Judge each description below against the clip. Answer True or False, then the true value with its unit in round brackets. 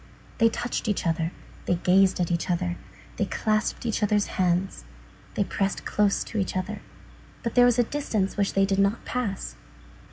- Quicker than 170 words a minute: True (180 wpm)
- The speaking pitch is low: False (200 Hz)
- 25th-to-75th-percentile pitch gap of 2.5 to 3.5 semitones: True (2.9 semitones)